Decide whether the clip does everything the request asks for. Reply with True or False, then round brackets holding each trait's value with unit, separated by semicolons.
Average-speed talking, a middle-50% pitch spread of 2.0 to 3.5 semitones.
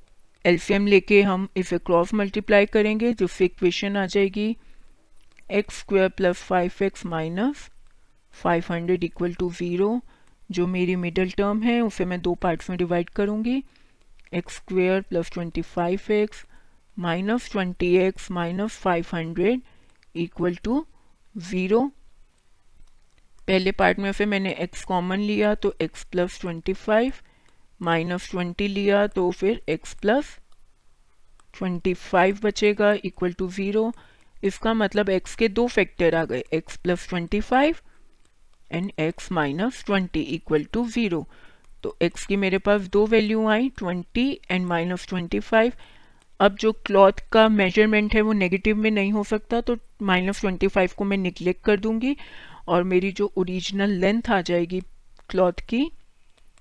True (145 wpm; 3.0 semitones)